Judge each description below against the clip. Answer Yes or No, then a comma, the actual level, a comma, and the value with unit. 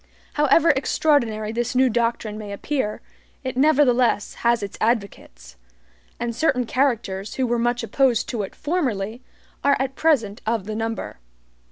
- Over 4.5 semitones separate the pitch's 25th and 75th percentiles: No, average, 3.6 semitones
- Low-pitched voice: No, high, 235 Hz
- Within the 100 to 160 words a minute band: Yes, average, 145 wpm